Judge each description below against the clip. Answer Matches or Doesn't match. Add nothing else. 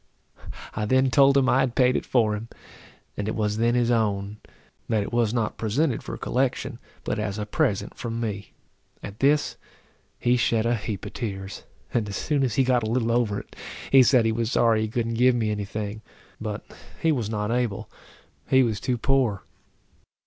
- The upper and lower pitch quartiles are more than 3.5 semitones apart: Doesn't match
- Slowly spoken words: Doesn't match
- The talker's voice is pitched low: Matches